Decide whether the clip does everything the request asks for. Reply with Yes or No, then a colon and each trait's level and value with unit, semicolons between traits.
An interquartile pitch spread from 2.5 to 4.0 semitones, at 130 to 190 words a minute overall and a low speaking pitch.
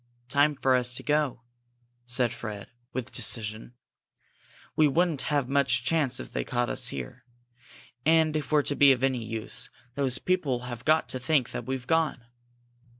Yes: average, 3.5 semitones; average, 165 wpm; low, 130 Hz